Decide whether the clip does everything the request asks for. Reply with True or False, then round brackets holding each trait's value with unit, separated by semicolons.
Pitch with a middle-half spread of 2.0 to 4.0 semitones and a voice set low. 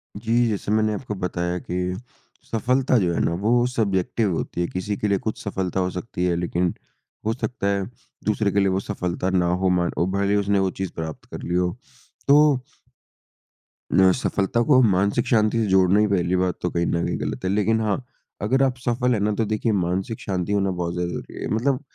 True (3.5 semitones; 100 Hz)